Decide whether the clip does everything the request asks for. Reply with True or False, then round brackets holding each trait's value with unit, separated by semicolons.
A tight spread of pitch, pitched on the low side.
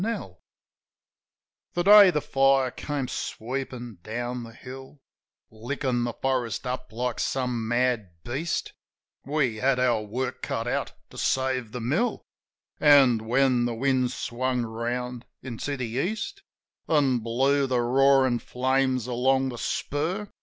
True (2.1 semitones; 125 Hz)